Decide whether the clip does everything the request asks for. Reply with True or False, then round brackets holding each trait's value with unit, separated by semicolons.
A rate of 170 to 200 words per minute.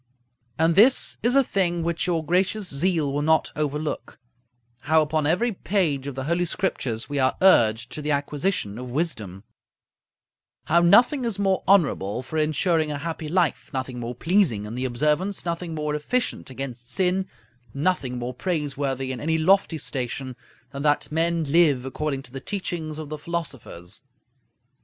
False (160 wpm)